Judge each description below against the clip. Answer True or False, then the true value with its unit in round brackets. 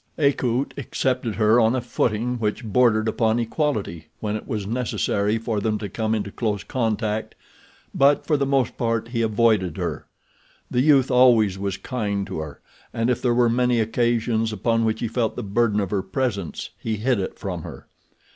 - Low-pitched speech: True (115 Hz)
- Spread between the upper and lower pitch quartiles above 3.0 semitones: False (2.6 semitones)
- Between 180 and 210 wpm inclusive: True (185 wpm)